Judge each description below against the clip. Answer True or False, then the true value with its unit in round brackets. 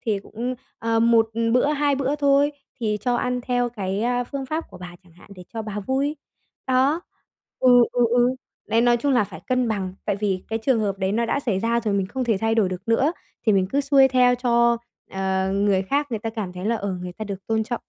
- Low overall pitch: False (230 Hz)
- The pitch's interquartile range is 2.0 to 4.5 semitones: True (4.1 semitones)